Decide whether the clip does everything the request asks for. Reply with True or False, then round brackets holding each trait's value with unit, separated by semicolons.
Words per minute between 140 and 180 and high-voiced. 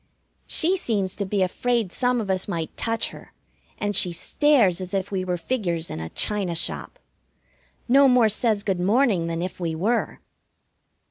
True (175 wpm; 200 Hz)